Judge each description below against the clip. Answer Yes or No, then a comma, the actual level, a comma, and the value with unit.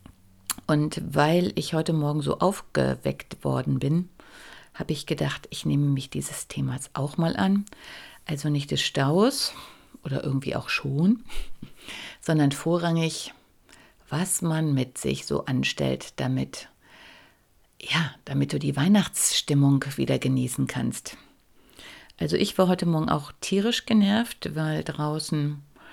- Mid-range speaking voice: Yes, medium, 150 Hz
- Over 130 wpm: No, slow, 125 wpm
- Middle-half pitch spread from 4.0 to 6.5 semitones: Yes, average, 5.2 semitones